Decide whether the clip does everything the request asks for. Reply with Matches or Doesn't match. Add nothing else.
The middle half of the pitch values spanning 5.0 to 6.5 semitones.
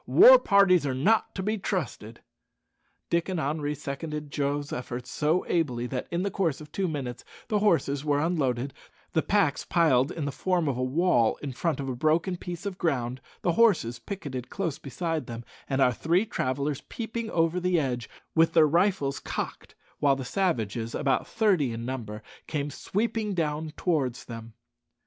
Matches